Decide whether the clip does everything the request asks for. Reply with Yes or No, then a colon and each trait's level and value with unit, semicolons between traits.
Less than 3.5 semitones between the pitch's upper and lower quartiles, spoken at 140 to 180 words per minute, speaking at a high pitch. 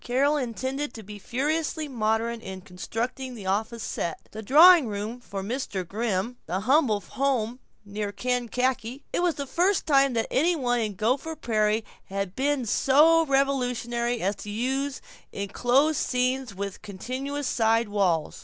No: average, 4.5 semitones; average, 155 wpm; high, 240 Hz